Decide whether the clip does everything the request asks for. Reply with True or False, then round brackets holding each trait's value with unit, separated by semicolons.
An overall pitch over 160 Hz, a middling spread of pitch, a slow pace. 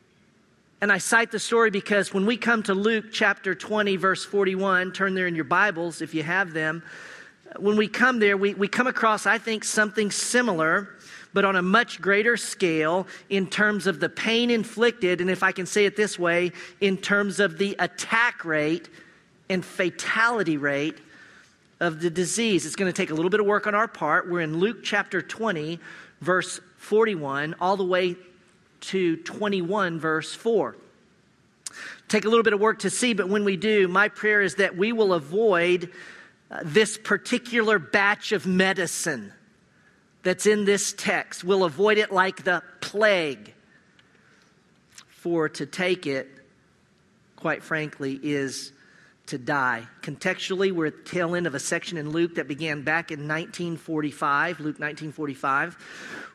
False (190 Hz; 3.6 semitones; 165 wpm)